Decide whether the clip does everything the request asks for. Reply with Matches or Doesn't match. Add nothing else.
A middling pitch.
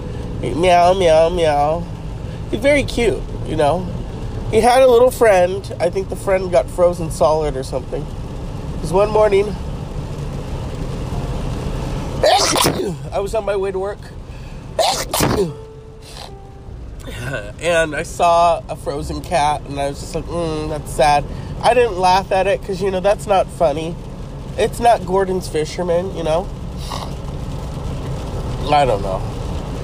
Matches